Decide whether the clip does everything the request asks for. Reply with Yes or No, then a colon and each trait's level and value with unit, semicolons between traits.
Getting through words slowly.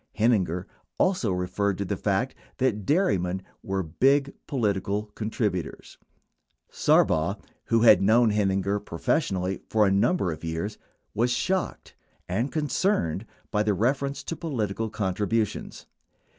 Yes: slow, 130 wpm